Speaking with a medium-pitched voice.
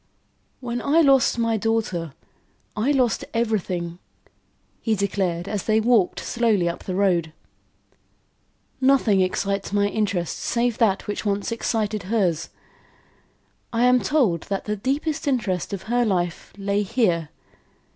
No: high, 210 Hz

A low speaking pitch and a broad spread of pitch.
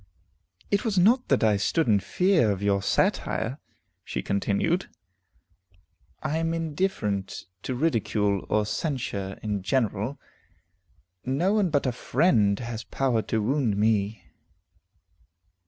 Yes: low, 120 Hz; wide, 7.9 semitones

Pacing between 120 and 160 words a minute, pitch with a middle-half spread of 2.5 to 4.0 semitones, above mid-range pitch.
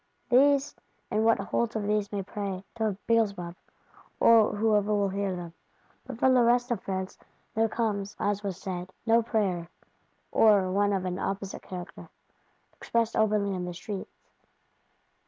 Yes: average, 150 wpm; average, 2.9 semitones; high, 205 Hz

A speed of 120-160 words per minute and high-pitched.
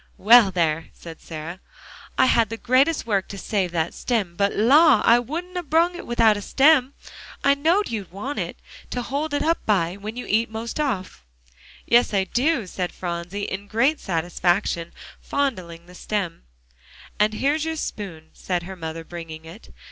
No: average, 180 wpm; high, 210 Hz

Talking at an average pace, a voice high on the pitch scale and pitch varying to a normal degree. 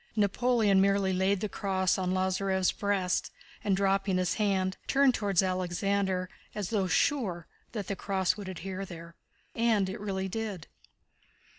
No: average, 145 wpm; high, 195 Hz; narrow, 1.5 semitones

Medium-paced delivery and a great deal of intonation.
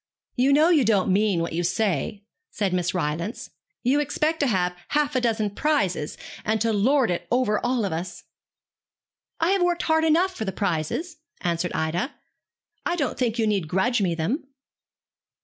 Yes: average, 175 wpm; wide, 7.9 semitones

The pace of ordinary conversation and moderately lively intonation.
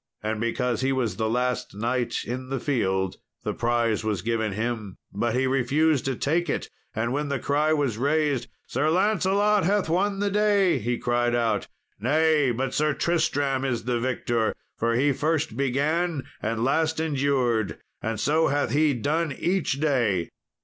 Yes: average, 165 wpm; average, 4.8 semitones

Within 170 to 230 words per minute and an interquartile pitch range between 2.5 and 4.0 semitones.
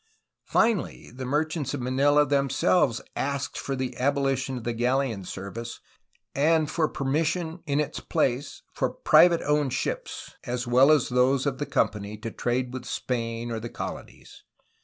No: average, 155 wpm; average, 3.2 semitones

